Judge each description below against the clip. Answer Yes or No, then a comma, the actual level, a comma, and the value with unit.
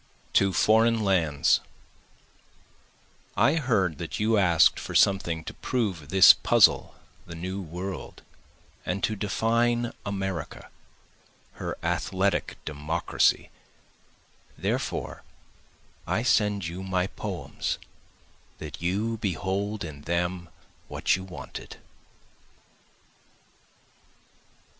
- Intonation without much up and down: No, average, 3.7 semitones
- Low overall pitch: Yes, very low, 95 Hz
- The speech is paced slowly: Yes, slow, 90 wpm